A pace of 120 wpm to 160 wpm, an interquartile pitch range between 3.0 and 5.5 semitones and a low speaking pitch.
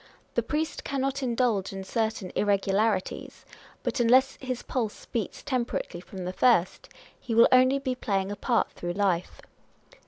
No: average, 150 wpm; average, 4.8 semitones; high, 225 Hz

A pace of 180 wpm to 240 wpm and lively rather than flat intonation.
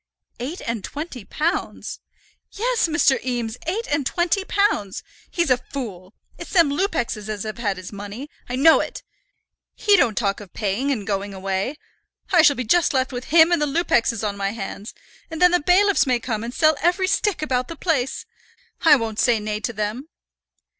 Yes: average, 190 wpm; wide, 7.5 semitones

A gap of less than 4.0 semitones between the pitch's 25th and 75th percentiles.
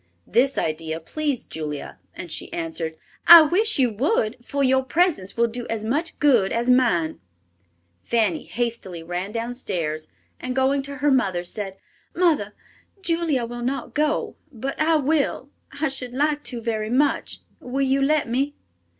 No: wide, 5.5 semitones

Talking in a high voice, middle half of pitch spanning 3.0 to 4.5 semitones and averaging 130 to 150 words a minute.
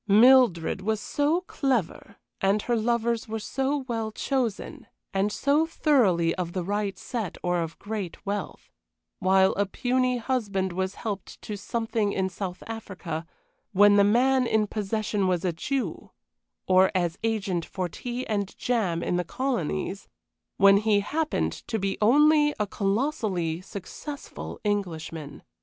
Yes: high, 205 Hz; average, 4.2 semitones; average, 145 wpm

